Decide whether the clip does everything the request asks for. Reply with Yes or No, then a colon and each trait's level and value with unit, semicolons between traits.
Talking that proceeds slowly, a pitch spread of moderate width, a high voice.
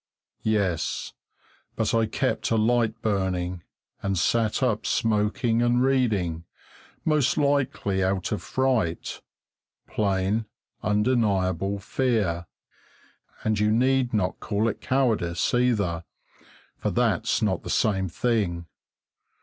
No: slow, 110 wpm; average, 4.1 semitones; low, 105 Hz